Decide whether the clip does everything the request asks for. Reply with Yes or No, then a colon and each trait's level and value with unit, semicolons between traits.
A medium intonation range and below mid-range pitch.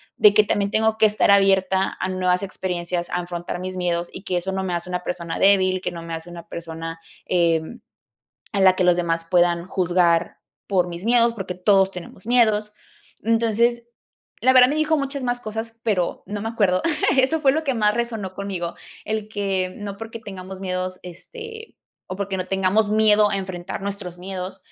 No: average, 3.4 semitones; high, 190 Hz